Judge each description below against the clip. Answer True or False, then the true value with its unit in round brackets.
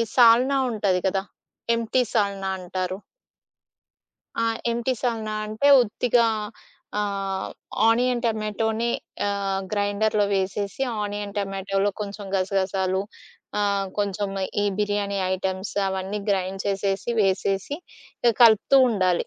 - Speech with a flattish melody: True (2.1 semitones)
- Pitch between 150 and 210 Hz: True (200 Hz)